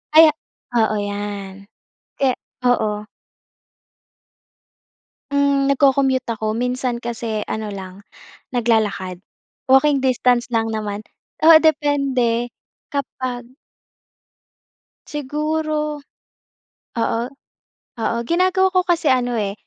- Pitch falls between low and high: No, high, 245 Hz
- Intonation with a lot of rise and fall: No, average, 4.5 semitones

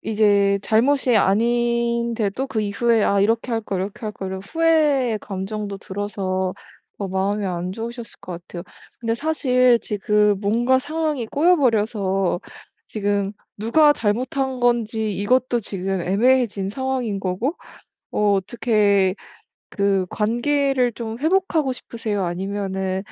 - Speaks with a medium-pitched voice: No, high, 220 Hz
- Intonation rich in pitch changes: No, average, 3.8 semitones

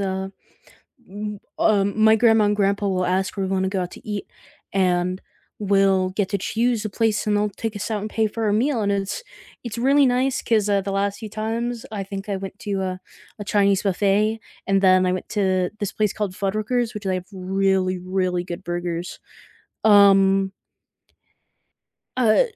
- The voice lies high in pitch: Yes, high, 200 Hz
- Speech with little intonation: Yes, narrow, 2.2 semitones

